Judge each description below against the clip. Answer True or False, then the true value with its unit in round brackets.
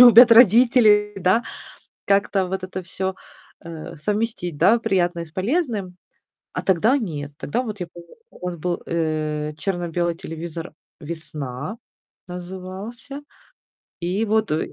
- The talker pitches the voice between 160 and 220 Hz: True (185 Hz)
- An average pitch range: True (4.1 semitones)